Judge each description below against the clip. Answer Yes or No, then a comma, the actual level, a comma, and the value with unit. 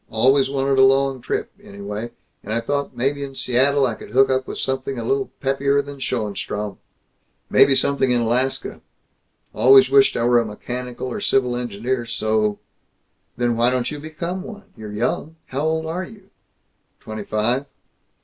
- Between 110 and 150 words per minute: No, average, 170 wpm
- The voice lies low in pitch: Yes, low, 130 Hz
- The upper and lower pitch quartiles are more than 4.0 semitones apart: No, average, 3.0 semitones